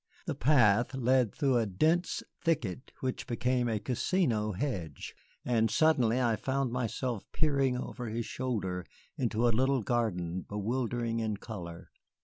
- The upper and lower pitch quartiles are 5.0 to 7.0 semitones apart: No, average, 3.3 semitones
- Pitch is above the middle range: No, low, 120 Hz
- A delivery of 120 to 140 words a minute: Yes, slow, 135 wpm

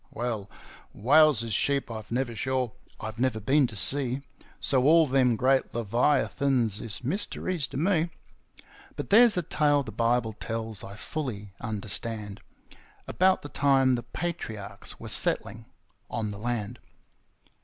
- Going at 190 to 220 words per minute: No, average, 140 wpm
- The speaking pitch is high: No, low, 125 Hz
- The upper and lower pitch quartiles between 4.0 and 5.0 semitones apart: Yes, average, 4.3 semitones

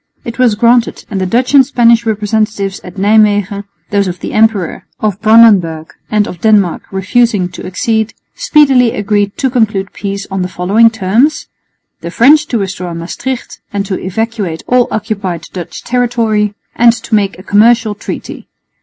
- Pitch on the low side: No, high, 210 Hz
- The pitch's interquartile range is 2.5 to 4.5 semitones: Yes, average, 3.2 semitones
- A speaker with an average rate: Yes, average, 160 wpm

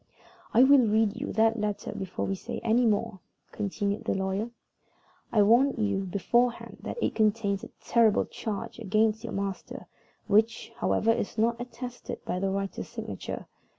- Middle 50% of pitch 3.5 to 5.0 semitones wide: No, narrow, 2.6 semitones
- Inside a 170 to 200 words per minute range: No, average, 155 wpm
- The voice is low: No, high, 220 Hz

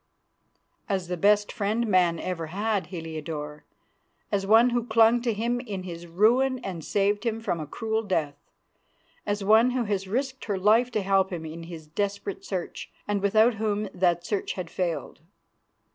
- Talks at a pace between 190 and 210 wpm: No, average, 170 wpm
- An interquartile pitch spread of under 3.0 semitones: No, average, 4.0 semitones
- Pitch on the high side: Yes, high, 200 Hz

